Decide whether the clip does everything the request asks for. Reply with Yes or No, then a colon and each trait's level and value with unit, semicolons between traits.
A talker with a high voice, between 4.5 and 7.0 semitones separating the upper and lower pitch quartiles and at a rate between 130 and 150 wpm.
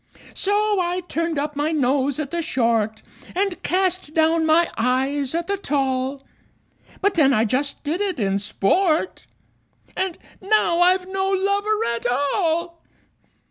Yes: very high, 325 Hz; wide, 5.5 semitones; average, 140 wpm